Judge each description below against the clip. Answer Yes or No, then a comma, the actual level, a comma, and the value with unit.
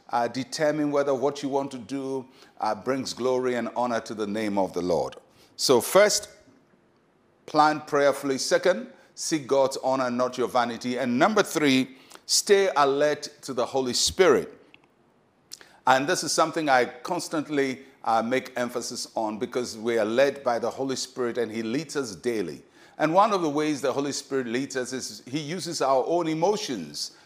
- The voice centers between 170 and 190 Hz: No, low, 135 Hz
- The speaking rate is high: No, average, 170 wpm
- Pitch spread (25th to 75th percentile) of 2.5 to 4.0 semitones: Yes, average, 3.1 semitones